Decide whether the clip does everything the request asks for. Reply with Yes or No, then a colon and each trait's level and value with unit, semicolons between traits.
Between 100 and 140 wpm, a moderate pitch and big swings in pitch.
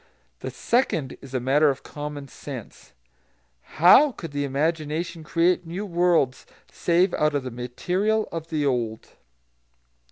No: slow, 135 wpm; medium, 155 Hz; average, 4.1 semitones